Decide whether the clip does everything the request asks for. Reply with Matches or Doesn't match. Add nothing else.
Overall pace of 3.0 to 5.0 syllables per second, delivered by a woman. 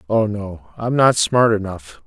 Doesn't match